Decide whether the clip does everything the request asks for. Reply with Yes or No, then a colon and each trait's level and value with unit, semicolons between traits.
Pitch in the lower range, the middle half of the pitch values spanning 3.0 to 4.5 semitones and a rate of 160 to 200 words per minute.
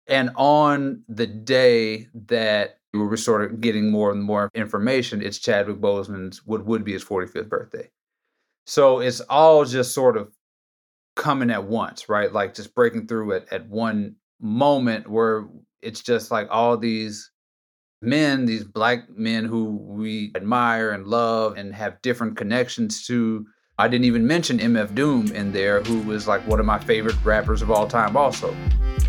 Yes: low, 115 Hz; average, 3.3 semitones; average, 170 wpm